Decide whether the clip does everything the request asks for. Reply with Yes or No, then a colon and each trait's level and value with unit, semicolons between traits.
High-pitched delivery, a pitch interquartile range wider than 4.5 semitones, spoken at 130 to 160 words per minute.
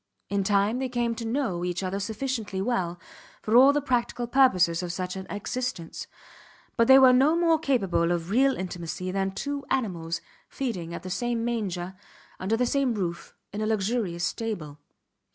No: high, 215 Hz; wide, 5.5 semitones; average, 170 wpm